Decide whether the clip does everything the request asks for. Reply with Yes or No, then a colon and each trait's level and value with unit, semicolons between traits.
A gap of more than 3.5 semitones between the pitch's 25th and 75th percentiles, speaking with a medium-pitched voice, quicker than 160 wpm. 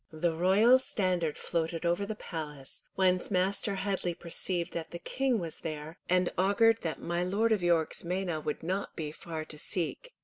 No: average, 3.2 semitones; medium, 175 Hz; average, 175 wpm